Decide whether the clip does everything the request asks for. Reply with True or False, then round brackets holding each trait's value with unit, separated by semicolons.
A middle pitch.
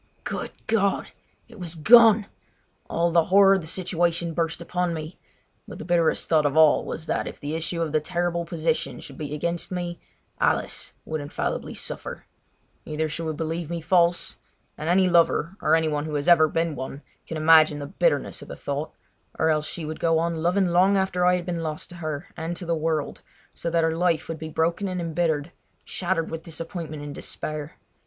True (165 Hz)